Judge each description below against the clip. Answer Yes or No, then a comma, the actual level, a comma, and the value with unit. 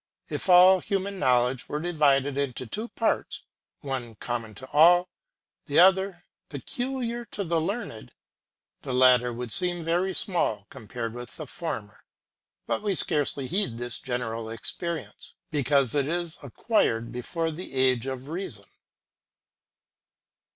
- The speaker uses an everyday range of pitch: No, wide, 6.4 semitones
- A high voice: No, medium, 145 Hz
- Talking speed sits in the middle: No, slow, 130 wpm